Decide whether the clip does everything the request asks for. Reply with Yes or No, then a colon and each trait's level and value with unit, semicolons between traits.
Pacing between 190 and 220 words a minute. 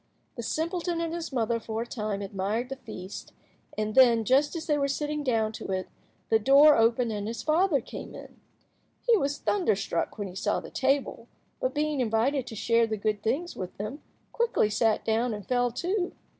Yes: average, 195 wpm